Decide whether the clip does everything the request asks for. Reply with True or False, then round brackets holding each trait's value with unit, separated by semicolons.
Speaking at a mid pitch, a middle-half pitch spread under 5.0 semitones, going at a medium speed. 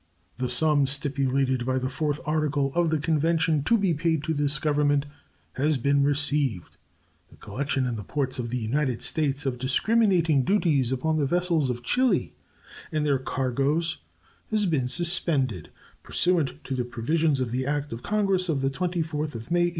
True (145 Hz; 3.6 semitones; 175 wpm)